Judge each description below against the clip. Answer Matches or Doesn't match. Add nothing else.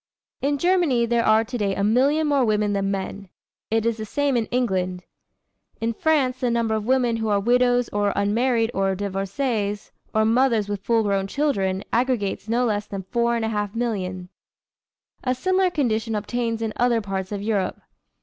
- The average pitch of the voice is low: Doesn't match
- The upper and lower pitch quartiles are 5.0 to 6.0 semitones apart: Doesn't match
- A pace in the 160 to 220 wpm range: Matches